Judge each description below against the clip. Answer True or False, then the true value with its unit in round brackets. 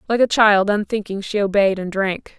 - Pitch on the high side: True (205 Hz)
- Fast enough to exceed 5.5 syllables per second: False (5.0 syllables/s)